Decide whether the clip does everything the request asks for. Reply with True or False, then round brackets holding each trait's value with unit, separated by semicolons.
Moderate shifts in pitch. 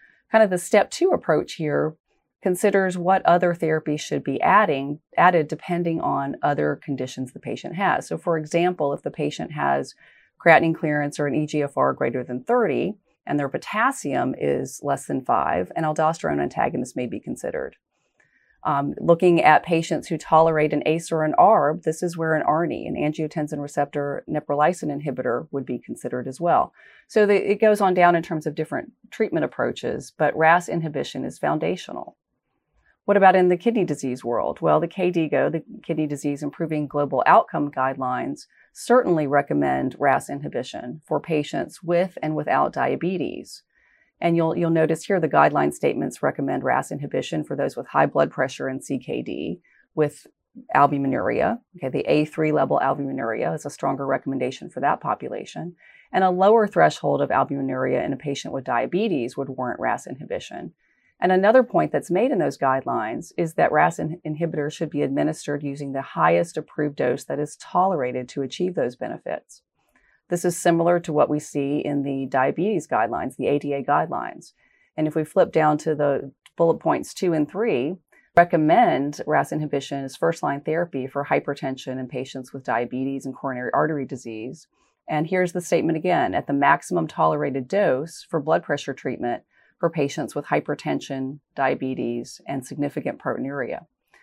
True (3.7 semitones)